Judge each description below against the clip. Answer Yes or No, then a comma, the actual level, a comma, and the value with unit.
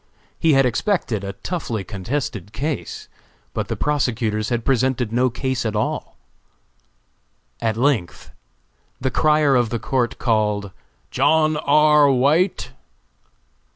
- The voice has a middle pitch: No, low, 125 Hz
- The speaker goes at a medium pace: No, slow, 120 wpm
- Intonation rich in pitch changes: No, average, 4.9 semitones